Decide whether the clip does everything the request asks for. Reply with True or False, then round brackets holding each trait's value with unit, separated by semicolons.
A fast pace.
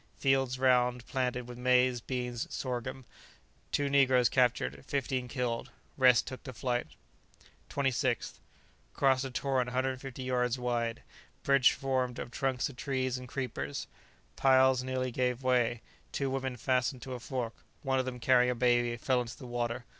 False (155 wpm)